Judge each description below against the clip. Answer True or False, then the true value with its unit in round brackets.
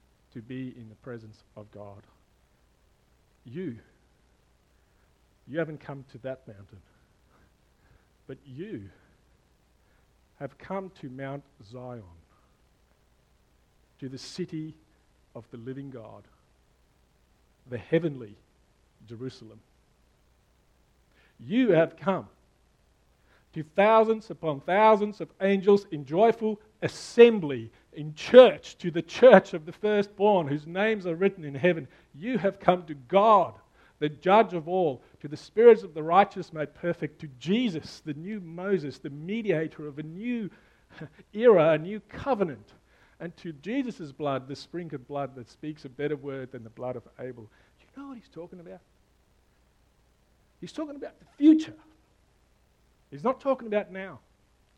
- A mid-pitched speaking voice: True (155 Hz)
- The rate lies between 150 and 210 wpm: False (135 wpm)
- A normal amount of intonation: False (7.9 semitones)